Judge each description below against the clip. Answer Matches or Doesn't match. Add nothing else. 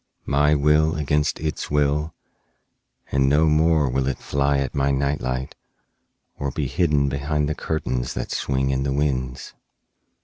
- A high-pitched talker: Doesn't match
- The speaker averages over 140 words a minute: Matches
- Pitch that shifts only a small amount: Matches